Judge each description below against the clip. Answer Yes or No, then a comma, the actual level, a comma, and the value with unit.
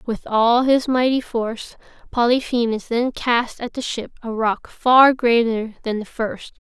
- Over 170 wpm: No, average, 160 wpm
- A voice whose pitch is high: Yes, high, 235 Hz